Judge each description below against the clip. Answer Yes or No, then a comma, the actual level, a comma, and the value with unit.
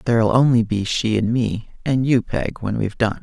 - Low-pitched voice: Yes, low, 115 Hz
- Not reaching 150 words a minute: No, fast, 205 wpm